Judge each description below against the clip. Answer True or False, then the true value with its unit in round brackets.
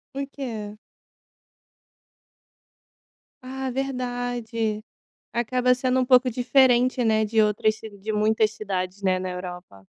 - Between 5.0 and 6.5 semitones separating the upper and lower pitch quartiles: False (3.1 semitones)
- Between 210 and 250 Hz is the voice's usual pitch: True (225 Hz)